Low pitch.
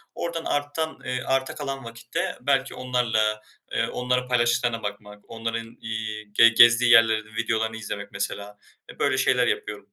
Yes: low, 115 Hz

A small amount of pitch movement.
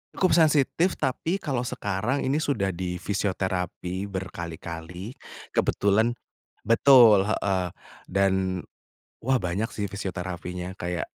No: average, 4.9 semitones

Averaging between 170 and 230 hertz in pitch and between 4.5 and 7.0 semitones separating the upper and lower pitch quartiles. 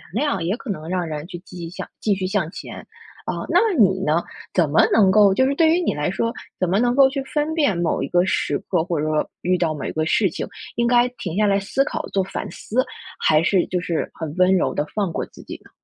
Yes: high, 190 Hz; wide, 5.5 semitones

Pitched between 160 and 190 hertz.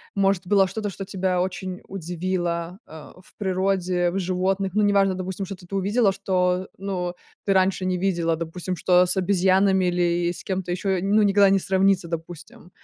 Yes: medium, 185 Hz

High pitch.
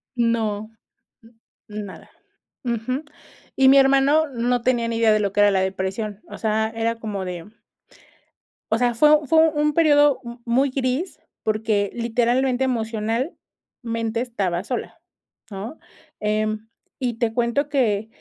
Yes: high, 230 Hz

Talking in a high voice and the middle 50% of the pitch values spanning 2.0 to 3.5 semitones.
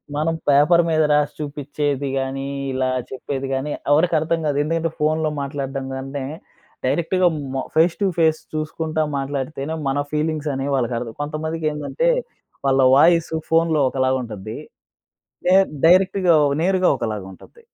No: medium, 150 Hz; average, 3.2 semitones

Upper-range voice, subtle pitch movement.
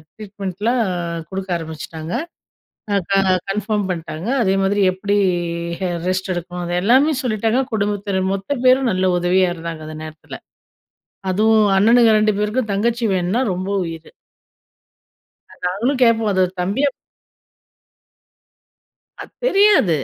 No: high, 200 Hz; average, 3.8 semitones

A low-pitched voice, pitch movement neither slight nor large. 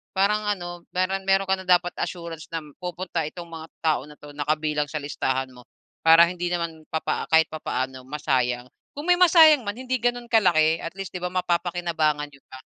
No: medium, 170 Hz; average, 3.9 semitones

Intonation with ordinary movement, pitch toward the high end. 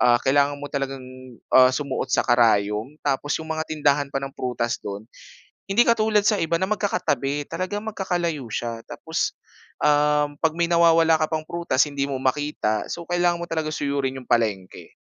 No: average, 4.2 semitones; medium, 145 Hz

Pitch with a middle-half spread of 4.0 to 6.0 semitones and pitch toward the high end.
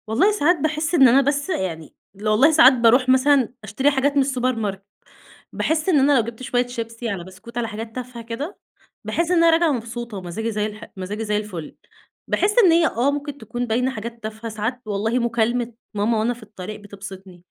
Yes: average, 4.4 semitones; high, 235 Hz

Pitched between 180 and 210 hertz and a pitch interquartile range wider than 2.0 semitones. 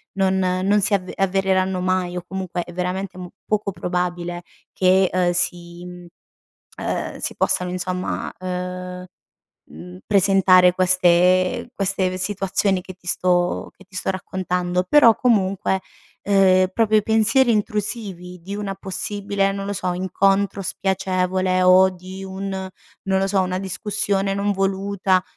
No: medium, 185 Hz; narrow, 1.3 semitones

